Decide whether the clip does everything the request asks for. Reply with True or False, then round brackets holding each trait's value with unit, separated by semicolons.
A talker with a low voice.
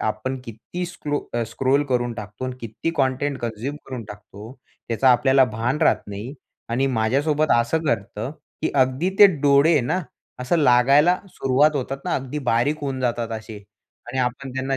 True (130 Hz)